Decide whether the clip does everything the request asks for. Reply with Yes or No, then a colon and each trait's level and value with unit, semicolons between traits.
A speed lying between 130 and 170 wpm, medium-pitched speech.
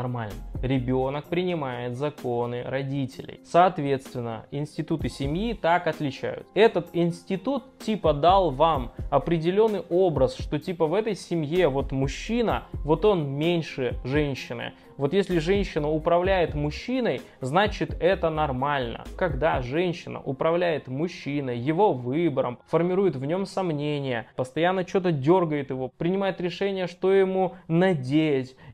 No: average, 115 wpm; medium, 160 Hz